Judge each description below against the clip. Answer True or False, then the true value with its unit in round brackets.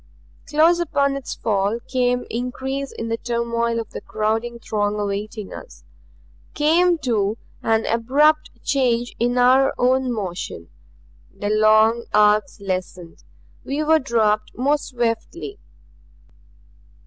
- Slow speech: True (115 wpm)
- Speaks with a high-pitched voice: True (235 Hz)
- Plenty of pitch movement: False (4.1 semitones)